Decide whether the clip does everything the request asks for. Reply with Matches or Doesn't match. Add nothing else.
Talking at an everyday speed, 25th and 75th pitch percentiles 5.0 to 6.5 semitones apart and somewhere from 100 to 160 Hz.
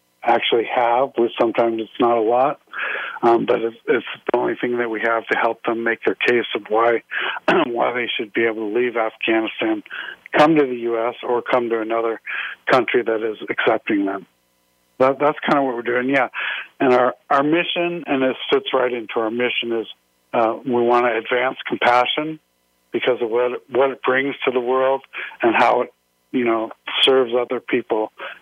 Doesn't match